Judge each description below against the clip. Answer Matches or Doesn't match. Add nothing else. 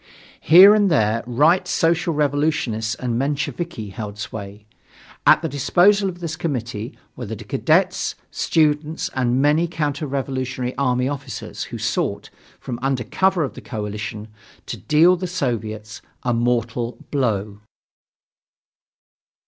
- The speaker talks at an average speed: Doesn't match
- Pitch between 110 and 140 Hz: Matches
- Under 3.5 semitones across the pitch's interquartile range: Doesn't match